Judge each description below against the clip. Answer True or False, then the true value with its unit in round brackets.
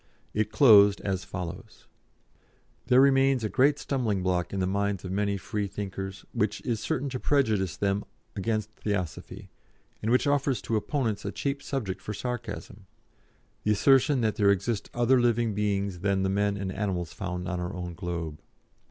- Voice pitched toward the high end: False (105 Hz)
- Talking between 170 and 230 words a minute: False (160 wpm)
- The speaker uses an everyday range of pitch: True (3.9 semitones)